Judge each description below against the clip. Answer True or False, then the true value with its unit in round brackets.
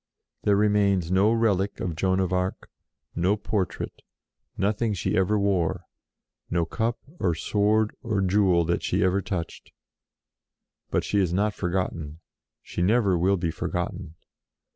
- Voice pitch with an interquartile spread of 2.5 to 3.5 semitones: True (2.8 semitones)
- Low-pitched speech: True (95 Hz)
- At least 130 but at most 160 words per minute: True (140 wpm)